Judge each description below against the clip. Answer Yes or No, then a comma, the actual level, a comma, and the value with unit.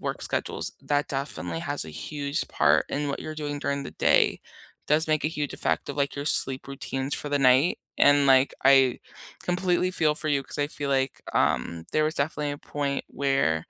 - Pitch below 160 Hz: Yes, medium, 140 Hz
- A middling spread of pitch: No, narrow, 1.9 semitones